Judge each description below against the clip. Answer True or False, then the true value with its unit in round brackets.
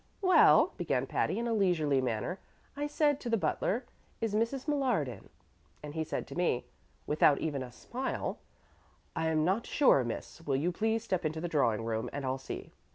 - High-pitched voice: False (170 Hz)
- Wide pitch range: True (8.8 semitones)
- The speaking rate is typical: True (190 wpm)